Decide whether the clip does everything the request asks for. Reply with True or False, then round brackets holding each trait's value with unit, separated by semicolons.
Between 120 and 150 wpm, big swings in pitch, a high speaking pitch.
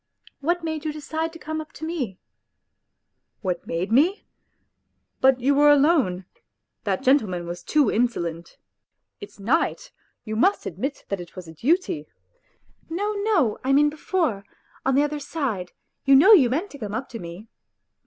False (180 wpm; 8.0 semitones; 275 Hz)